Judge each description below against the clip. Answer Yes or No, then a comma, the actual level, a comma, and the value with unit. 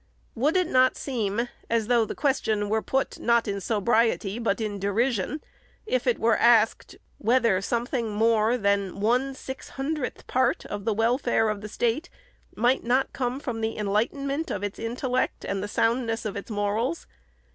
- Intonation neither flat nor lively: Yes, average, 3.3 semitones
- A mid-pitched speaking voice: No, high, 230 Hz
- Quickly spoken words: No, average, 170 wpm